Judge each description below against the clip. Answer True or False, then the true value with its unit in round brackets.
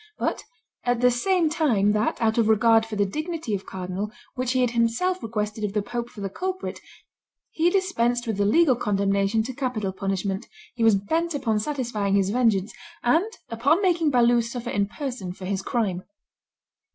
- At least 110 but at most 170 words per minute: False (180 wpm)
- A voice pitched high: True (230 Hz)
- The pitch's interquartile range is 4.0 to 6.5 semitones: True (4.4 semitones)